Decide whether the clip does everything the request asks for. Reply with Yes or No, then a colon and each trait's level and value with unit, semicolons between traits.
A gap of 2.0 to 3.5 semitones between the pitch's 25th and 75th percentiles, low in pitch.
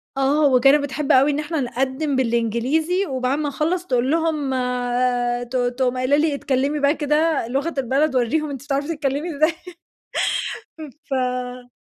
No: average, 3.2 semitones; very high, 275 Hz